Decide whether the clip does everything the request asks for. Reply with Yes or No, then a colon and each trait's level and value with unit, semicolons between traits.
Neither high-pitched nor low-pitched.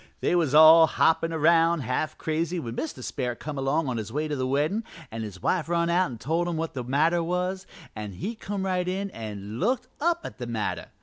Yes: medium, 160 Hz